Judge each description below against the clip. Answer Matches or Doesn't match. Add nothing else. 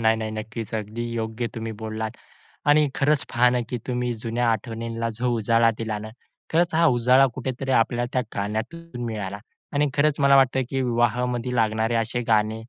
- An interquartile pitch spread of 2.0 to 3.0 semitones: Matches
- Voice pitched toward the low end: Matches